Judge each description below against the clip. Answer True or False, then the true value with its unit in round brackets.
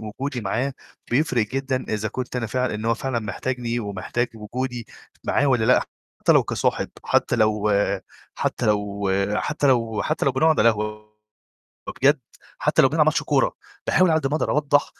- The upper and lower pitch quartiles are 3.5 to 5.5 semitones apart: True (4.2 semitones)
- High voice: False (120 Hz)